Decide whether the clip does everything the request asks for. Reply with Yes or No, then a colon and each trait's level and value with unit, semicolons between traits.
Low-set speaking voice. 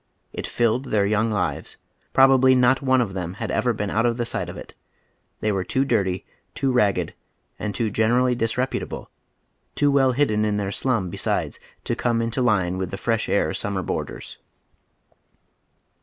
Yes: low, 115 Hz